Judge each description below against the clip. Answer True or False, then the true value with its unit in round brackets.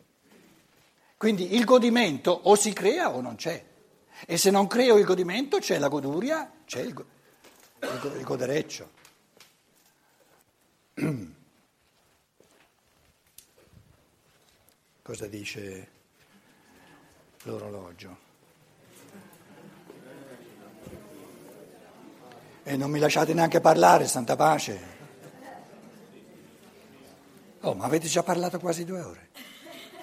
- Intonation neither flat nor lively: False (7.5 semitones)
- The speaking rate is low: True (90 wpm)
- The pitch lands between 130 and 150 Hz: False (175 Hz)